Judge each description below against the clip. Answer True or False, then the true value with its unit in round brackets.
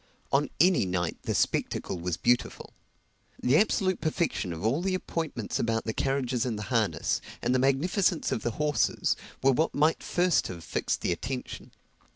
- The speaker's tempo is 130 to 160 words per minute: False (170 wpm)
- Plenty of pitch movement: True (6.5 semitones)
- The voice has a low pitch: True (130 Hz)